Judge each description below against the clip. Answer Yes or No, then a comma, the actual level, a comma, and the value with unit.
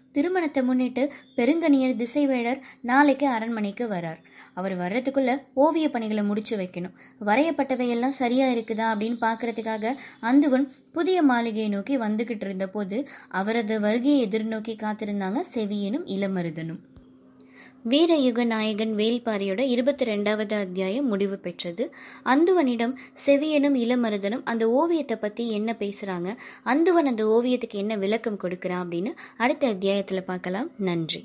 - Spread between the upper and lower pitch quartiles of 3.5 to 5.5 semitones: Yes, average, 4.4 semitones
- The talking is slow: No, average, 115 wpm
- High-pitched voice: Yes, high, 230 Hz